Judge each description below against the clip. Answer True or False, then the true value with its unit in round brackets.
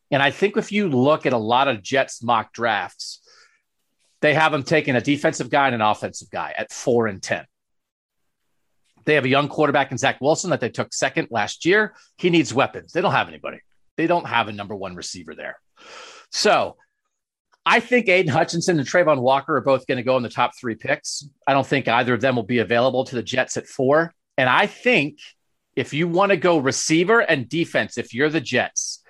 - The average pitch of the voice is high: False (140 Hz)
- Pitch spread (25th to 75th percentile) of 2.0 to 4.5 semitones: False (5.0 semitones)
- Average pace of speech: False (215 wpm)